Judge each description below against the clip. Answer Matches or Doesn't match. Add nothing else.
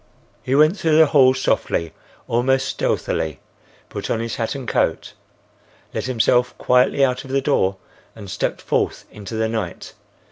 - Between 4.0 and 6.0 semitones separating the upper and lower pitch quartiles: Doesn't match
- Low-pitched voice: Matches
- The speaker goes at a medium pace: Matches